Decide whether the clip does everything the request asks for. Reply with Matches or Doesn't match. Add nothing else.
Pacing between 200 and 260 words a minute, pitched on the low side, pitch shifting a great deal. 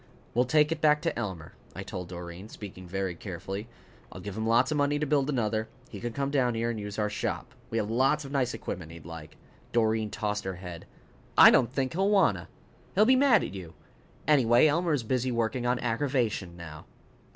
Matches